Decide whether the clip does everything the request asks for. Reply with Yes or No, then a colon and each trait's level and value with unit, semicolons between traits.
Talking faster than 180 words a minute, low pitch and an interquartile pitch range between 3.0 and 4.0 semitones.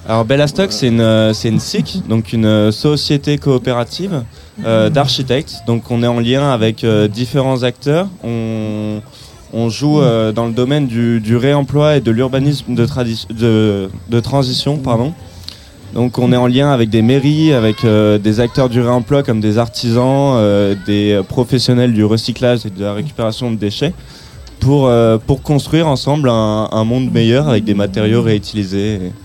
No: average, 165 wpm; low, 120 Hz; average, 3.7 semitones